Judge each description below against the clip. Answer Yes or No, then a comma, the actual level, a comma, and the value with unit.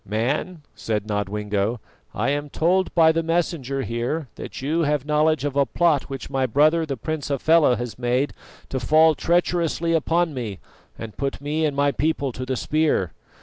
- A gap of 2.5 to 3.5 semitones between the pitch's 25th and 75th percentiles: No, average, 4.5 semitones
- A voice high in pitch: No, medium, 145 Hz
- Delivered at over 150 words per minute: Yes, average, 175 wpm